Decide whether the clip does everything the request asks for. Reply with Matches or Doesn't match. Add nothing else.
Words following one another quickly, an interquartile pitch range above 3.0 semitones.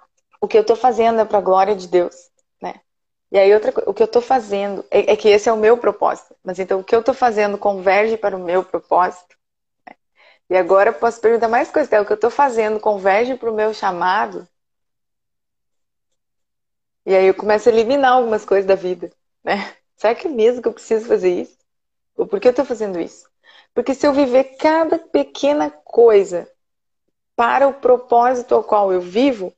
Matches